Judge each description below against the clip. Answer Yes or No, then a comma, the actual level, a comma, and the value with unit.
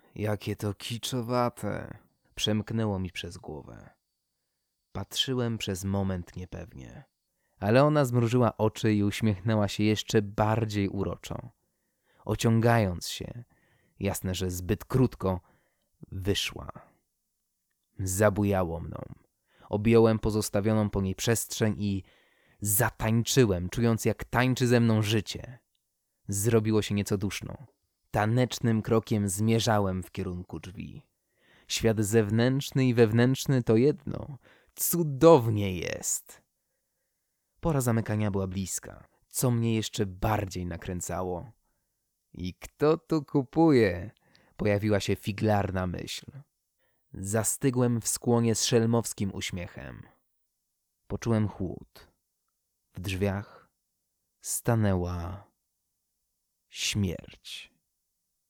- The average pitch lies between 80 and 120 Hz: Yes, low, 105 Hz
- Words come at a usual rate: No, slow, 90 wpm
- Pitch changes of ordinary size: Yes, average, 3.3 semitones